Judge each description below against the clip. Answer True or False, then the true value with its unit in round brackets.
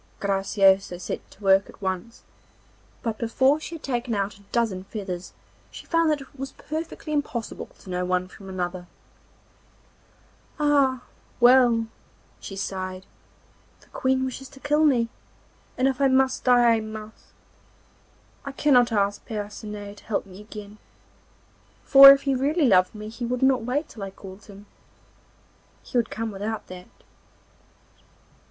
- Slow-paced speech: False (150 wpm)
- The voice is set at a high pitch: True (225 Hz)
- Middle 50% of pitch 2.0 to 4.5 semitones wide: False (5.0 semitones)